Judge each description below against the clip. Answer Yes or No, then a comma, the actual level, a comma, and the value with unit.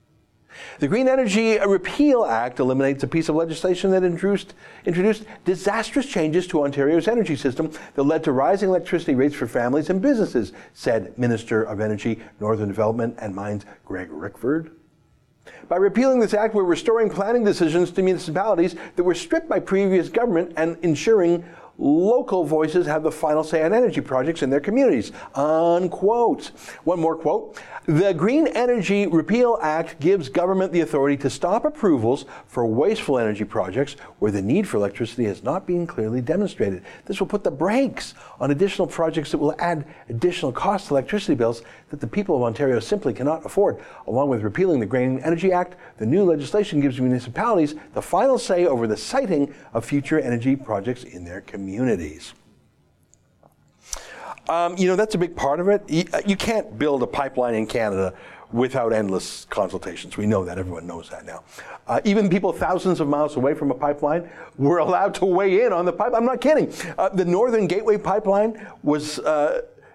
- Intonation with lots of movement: Yes, wide, 6.2 semitones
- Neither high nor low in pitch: Yes, medium, 170 Hz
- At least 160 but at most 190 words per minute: Yes, average, 170 wpm